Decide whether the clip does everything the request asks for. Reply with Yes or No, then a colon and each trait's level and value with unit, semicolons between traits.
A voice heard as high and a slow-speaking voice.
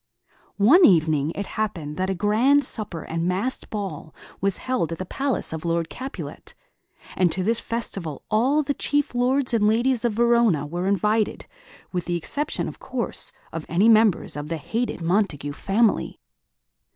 No: high, 200 Hz; average, 165 wpm